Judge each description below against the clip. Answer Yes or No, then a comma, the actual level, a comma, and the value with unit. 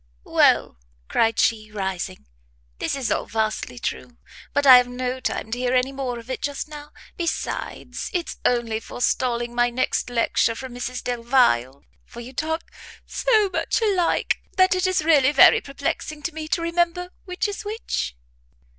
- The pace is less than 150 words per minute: No, average, 165 wpm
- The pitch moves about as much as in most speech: No, wide, 5.7 semitones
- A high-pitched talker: Yes, very high, 255 Hz